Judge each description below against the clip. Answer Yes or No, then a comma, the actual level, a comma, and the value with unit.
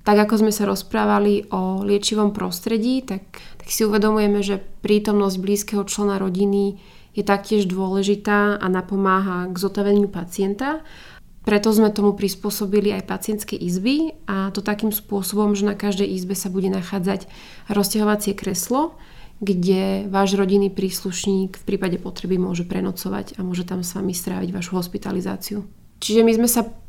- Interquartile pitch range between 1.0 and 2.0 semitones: Yes, narrow, 1.6 semitones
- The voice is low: No, high, 200 Hz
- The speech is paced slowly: No, average, 145 wpm